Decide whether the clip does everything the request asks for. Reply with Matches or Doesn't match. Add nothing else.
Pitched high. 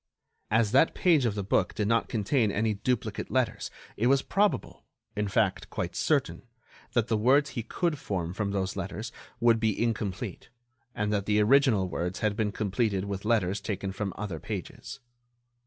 Doesn't match